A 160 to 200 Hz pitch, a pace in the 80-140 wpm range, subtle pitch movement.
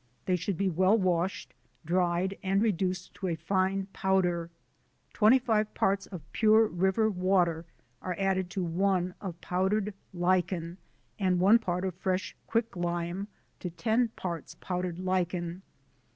Yes: medium, 185 Hz; slow, 135 wpm; narrow, 1.9 semitones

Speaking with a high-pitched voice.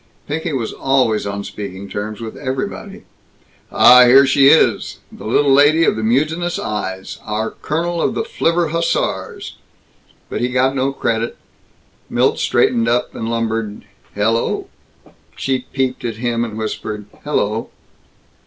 No: low, 120 Hz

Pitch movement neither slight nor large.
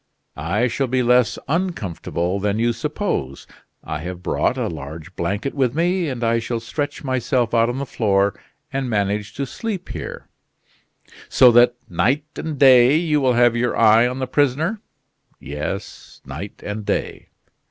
Yes: average, 5.0 semitones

